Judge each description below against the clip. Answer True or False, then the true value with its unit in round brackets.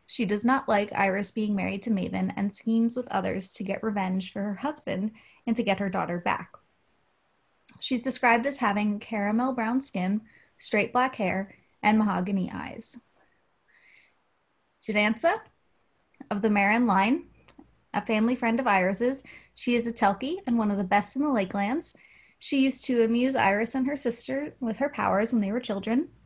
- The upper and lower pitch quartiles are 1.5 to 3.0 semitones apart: False (4.1 semitones)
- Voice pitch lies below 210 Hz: False (225 Hz)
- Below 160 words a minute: False (170 wpm)